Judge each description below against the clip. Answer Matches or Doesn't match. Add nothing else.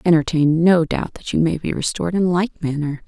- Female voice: Matches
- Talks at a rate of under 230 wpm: Doesn't match